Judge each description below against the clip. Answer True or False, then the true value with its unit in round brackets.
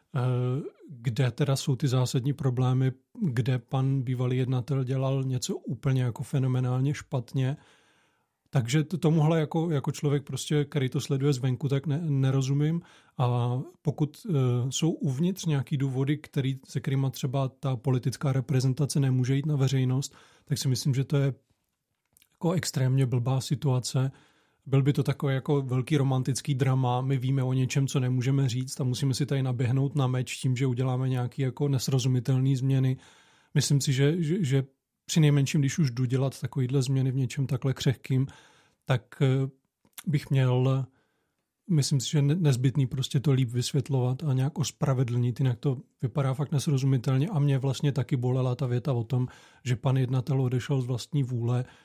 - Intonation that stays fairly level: True (1.7 semitones)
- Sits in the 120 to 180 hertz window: True (135 Hz)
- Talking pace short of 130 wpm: False (160 wpm)